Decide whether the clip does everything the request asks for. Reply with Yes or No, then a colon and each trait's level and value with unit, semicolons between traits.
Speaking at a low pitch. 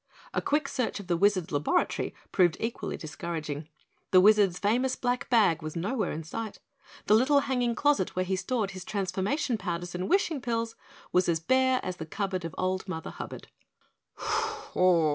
No: high, 195 Hz